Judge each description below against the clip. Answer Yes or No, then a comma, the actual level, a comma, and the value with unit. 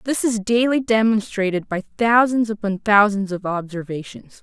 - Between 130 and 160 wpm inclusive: Yes, slow, 135 wpm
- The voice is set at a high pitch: Yes, high, 210 Hz